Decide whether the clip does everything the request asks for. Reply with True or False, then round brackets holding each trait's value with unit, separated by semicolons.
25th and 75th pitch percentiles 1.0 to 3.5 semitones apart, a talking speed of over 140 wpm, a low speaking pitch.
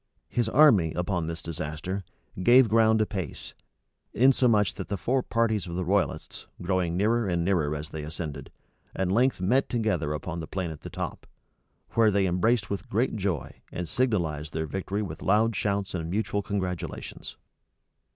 False (4.6 semitones; 160 wpm; 95 Hz)